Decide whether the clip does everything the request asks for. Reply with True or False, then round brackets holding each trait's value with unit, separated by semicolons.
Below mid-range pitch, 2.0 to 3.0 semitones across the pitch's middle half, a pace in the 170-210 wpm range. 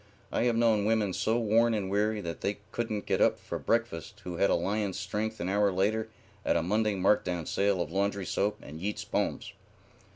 True (105 Hz; 2.5 semitones; 205 wpm)